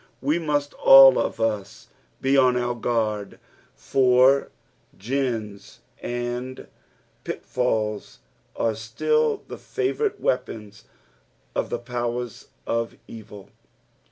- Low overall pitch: Yes, low, 120 Hz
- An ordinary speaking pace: No, slow, 100 wpm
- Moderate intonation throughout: Yes, average, 3.3 semitones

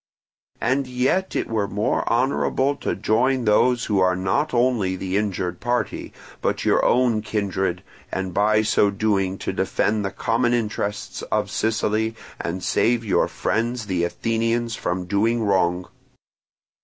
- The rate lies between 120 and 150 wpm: Yes, average, 145 wpm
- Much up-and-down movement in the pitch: No, average, 3.6 semitones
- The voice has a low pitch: Yes, low, 110 Hz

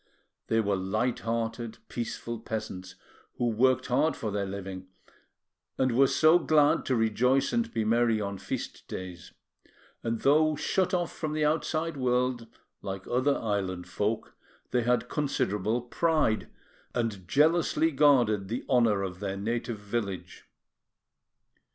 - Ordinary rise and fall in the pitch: Yes, average, 5.0 semitones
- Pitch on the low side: Yes, low, 115 Hz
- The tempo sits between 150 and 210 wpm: No, slow, 135 wpm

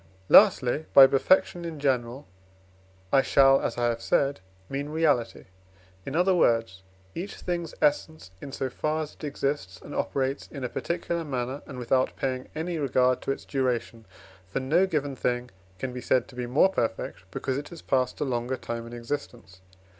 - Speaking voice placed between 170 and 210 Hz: No, low, 135 Hz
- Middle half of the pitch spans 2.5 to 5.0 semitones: Yes, average, 3.5 semitones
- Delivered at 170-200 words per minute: Yes, average, 175 wpm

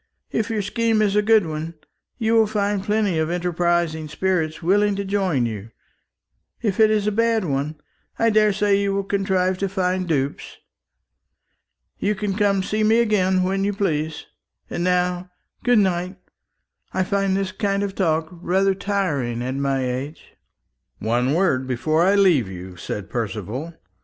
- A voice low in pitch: No, medium, 185 Hz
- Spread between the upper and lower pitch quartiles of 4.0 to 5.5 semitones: Yes, average, 4.5 semitones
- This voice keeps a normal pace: Yes, average, 160 wpm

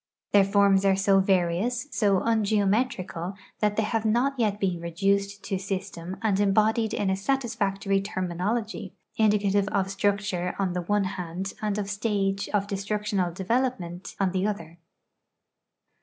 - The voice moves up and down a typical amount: No, narrow, 1.7 semitones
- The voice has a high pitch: Yes, high, 200 Hz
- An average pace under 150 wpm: Yes, average, 140 wpm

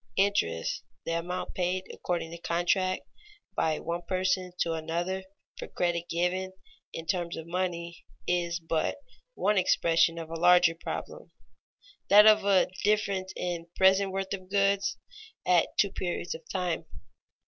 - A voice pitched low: No, medium, 180 Hz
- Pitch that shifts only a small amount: Yes, narrow, 2.0 semitones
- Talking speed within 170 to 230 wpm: No, average, 140 wpm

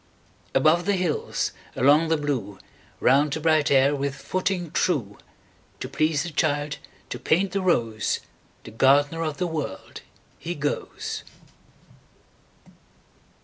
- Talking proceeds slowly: Yes, slow, 110 wpm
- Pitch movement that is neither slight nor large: Yes, average, 3.1 semitones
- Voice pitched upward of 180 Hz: No, medium, 150 Hz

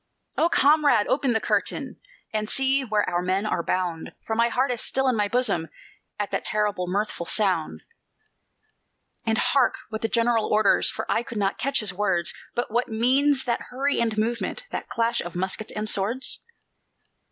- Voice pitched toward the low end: No, high, 220 Hz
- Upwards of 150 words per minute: Yes, average, 175 wpm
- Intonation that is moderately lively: Yes, average, 3.8 semitones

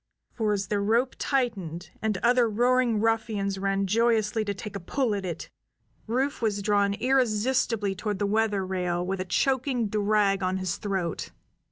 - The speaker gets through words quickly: No, average, 165 wpm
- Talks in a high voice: Yes, high, 210 Hz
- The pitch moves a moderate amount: Yes, average, 3.0 semitones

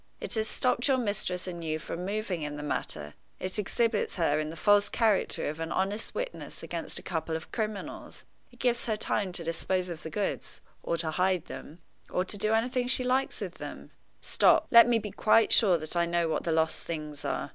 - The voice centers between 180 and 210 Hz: Yes, medium, 185 Hz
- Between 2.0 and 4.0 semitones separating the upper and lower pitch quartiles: No, average, 5.2 semitones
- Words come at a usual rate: No, fast, 215 wpm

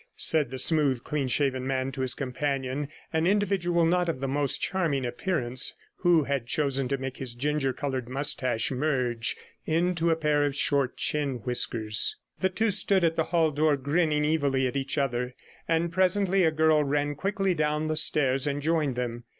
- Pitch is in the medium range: Yes, medium, 145 Hz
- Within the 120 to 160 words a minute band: No, average, 180 wpm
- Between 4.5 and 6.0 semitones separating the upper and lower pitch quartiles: No, average, 3.7 semitones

